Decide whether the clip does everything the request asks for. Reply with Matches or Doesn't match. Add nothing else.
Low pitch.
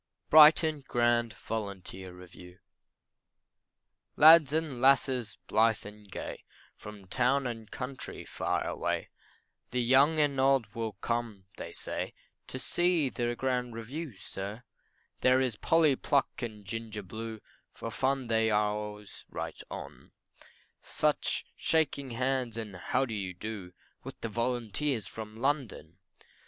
Matches